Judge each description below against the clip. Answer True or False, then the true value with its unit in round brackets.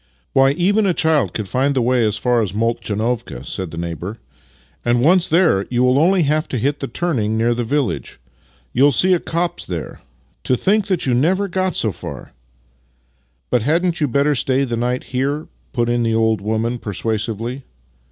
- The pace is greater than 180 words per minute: True (200 wpm)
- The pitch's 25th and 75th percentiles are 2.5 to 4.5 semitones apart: False (5.4 semitones)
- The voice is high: False (125 Hz)